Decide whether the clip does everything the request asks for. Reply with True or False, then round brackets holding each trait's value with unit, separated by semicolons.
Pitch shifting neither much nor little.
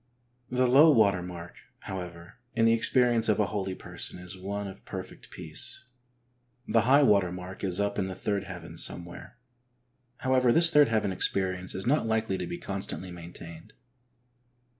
True (4.7 semitones)